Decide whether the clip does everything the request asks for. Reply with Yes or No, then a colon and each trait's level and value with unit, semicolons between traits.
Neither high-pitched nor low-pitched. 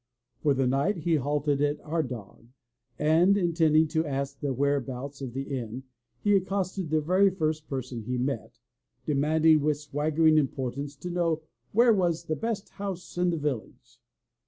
Yes: medium, 150 Hz